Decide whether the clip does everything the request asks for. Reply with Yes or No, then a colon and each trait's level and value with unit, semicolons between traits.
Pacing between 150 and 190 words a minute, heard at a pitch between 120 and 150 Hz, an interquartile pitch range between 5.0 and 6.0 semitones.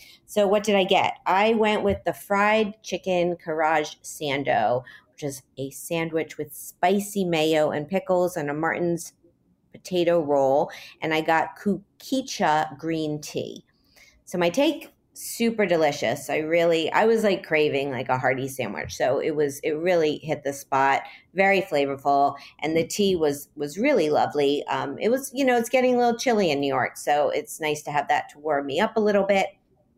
No: average, 180 wpm; medium, 165 Hz; wide, 5.4 semitones